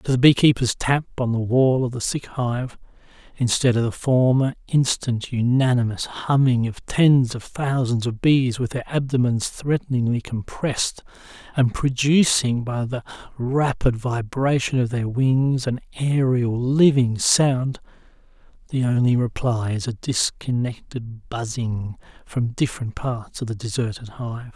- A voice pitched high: No, low, 125 Hz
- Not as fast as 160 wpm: Yes, slow, 135 wpm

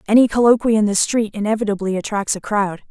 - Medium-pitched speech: No, high, 210 Hz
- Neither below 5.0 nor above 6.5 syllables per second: Yes, 6.3 syllables/s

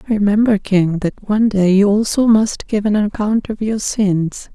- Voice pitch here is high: Yes, high, 205 Hz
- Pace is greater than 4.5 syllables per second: No, 4.4 syllables/s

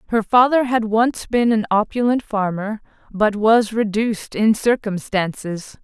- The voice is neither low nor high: No, high, 220 Hz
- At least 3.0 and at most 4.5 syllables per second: Yes, 4.2 syllables/s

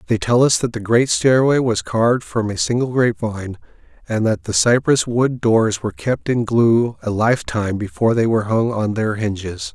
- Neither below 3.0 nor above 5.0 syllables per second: No, 5.2 syllables/s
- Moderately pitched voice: No, low, 115 Hz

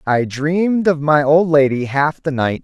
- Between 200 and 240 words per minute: Yes, fast, 205 wpm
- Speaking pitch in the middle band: Yes, medium, 150 Hz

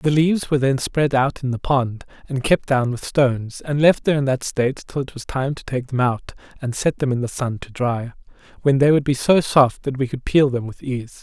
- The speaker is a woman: No, male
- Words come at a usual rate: No, fast, 260 wpm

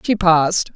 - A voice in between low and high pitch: Yes, medium, 175 Hz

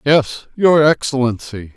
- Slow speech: Yes, slow, 100 wpm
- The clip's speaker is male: Yes, male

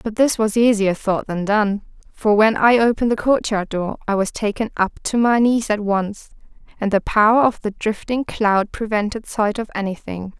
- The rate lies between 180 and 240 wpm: Yes, average, 195 wpm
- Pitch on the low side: No, high, 215 Hz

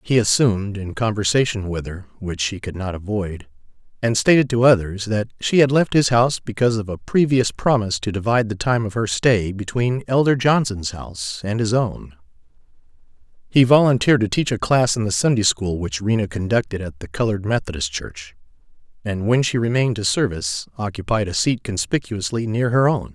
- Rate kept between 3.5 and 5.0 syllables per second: No, 5.5 syllables/s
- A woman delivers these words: No, male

